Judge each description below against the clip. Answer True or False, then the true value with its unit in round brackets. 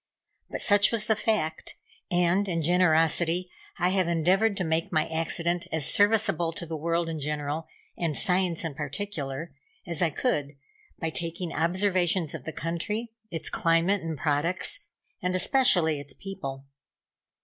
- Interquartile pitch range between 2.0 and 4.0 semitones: True (2.7 semitones)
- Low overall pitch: False (170 Hz)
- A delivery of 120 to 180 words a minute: True (150 wpm)